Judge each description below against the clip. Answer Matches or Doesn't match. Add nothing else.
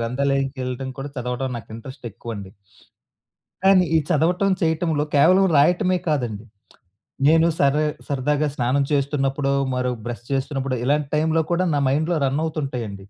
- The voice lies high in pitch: Doesn't match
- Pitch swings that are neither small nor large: Matches